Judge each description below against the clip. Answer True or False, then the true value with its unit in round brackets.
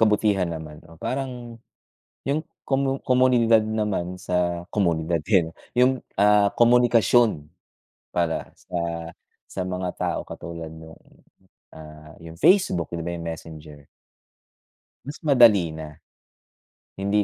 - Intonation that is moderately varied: False (6.3 semitones)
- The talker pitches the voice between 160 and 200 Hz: False (95 Hz)